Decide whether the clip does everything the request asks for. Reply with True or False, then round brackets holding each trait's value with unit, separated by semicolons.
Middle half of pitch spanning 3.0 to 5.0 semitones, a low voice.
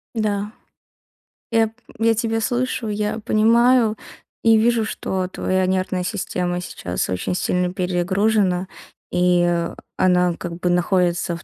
False (3.6 semitones; 190 Hz)